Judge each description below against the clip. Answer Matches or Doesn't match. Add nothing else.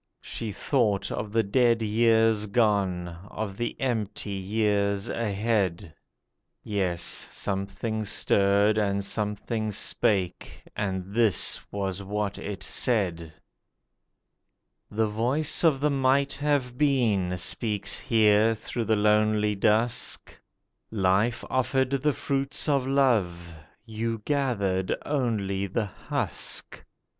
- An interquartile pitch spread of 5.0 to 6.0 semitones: Doesn't match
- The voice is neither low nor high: Doesn't match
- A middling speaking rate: Doesn't match